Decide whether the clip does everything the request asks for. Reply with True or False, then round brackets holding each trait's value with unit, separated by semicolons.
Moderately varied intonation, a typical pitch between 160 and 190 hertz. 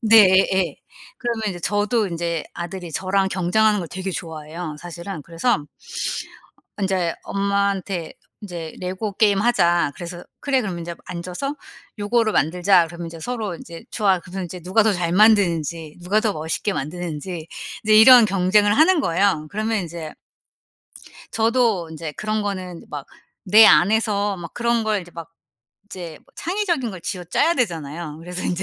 True (4.0 semitones; 185 Hz)